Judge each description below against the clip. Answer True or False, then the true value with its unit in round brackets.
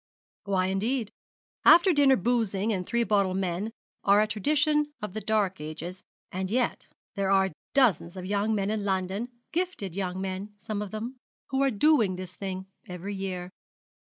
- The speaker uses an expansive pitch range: False (3.7 semitones)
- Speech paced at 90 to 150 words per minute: False (165 wpm)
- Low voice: False (200 Hz)